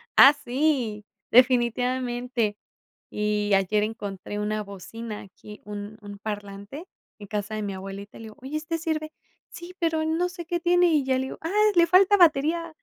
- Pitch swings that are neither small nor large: No, wide, 7.2 semitones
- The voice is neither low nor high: No, high, 240 Hz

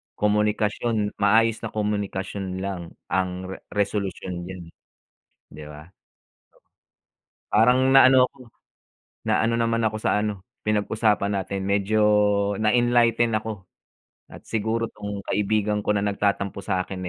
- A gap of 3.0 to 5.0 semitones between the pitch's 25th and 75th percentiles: No, narrow, 2.4 semitones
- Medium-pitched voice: No, low, 105 Hz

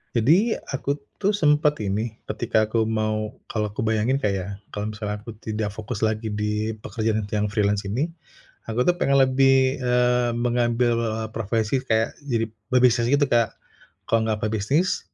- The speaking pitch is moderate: No, low, 110 Hz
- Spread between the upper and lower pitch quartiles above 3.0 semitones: No, average, 2.7 semitones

